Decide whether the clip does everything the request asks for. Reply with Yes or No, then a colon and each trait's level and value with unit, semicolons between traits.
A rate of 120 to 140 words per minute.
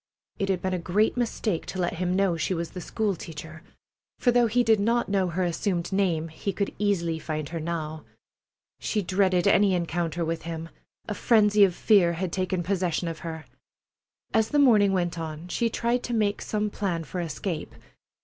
No: average, 190 wpm